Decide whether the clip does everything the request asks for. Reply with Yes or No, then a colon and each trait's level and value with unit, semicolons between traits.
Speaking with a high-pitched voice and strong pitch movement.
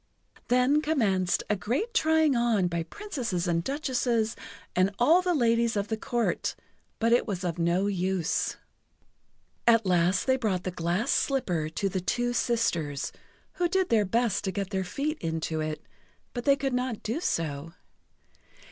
Yes: high, 220 Hz; wide, 5.9 semitones